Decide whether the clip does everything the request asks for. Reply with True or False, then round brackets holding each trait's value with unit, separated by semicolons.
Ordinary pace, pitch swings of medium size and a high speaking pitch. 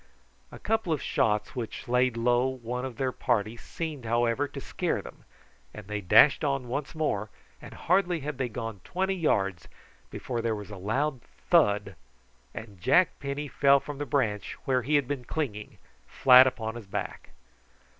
False (170 wpm; 4.5 semitones; 125 Hz)